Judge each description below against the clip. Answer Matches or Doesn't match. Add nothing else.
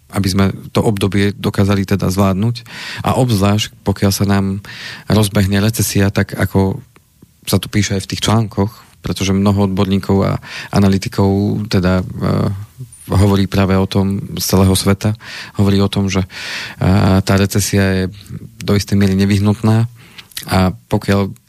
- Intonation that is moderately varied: Doesn't match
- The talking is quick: Doesn't match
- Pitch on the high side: Doesn't match